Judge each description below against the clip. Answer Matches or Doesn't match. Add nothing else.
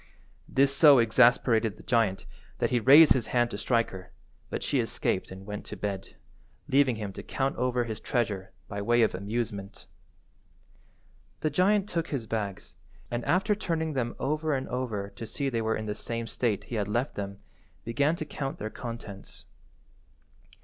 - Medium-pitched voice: Doesn't match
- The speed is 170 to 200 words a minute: Matches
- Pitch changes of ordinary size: Matches